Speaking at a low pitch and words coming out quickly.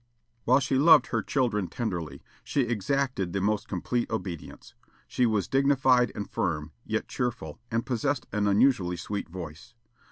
No: low, 115 Hz; average, 150 wpm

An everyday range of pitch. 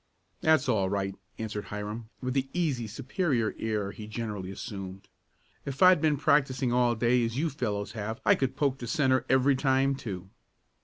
Yes: average, 4.3 semitones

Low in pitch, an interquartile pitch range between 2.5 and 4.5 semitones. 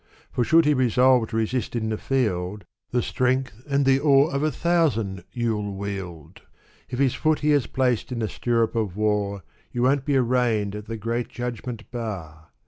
Yes: low, 120 Hz; average, 4.0 semitones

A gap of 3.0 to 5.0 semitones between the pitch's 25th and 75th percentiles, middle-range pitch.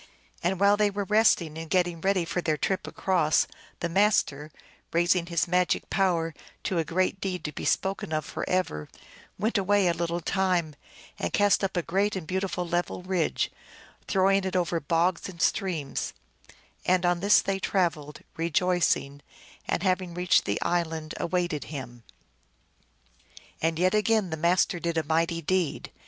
No: narrow, 2.6 semitones; medium, 175 Hz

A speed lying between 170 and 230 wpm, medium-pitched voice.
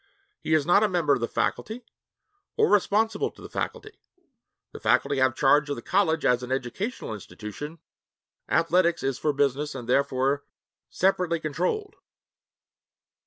No: average, 145 wpm; medium, 150 Hz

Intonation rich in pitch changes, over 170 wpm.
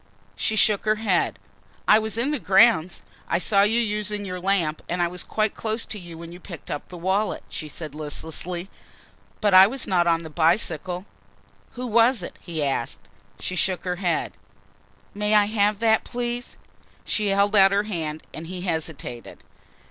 No: average, 3.9 semitones; average, 180 wpm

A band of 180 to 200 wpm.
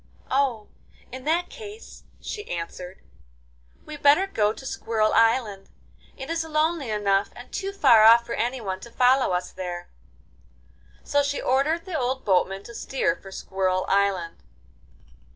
No: average, 150 wpm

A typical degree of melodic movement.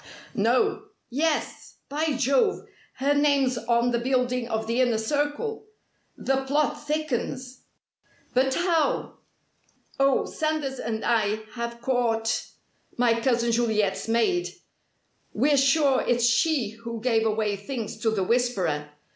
Yes: average, 3.8 semitones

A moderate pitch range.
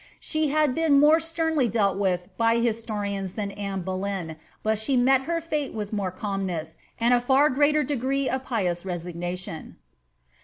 No: wide, 6.4 semitones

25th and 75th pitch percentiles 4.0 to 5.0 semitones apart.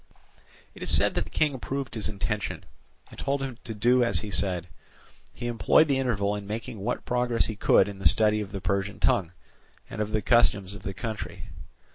No: average, 3.2 semitones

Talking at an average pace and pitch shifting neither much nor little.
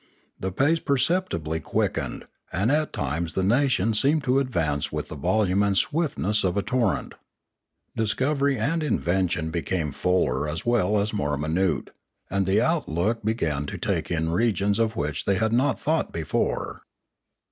No: average, 160 wpm; wide, 7.2 semitones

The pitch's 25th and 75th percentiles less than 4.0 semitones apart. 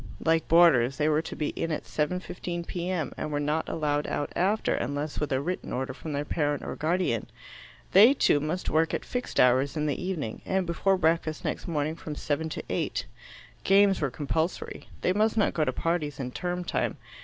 Yes: average, 3.4 semitones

